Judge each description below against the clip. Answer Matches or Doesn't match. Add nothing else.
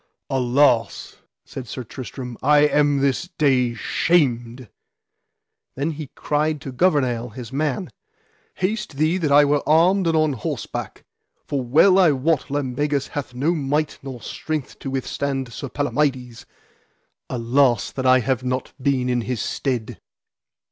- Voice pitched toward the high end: Doesn't match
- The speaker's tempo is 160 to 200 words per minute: Doesn't match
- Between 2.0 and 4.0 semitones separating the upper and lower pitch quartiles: Matches